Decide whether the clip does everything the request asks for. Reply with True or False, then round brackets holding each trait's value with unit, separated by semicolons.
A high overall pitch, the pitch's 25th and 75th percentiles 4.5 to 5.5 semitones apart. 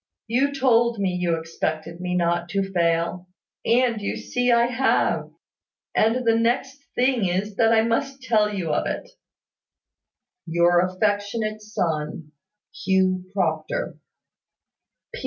True (205 Hz; 5.1 semitones)